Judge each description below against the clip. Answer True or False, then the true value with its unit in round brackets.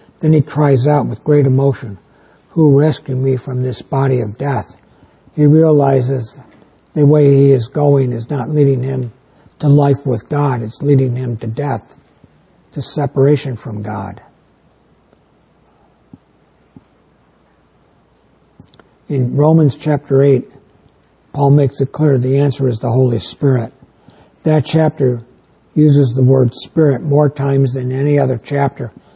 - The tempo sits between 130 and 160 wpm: True (135 wpm)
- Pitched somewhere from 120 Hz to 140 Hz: True (135 Hz)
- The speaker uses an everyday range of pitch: False (2.2 semitones)